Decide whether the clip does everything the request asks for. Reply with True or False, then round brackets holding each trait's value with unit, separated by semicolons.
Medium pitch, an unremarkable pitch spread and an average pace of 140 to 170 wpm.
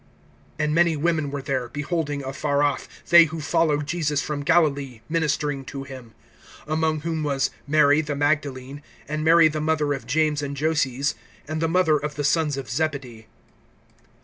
False (150 Hz; 2.0 semitones; 165 wpm)